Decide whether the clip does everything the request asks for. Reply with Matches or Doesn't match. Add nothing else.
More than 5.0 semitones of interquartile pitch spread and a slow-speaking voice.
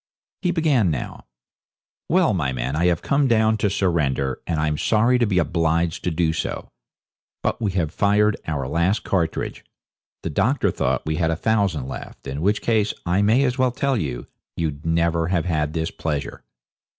Doesn't match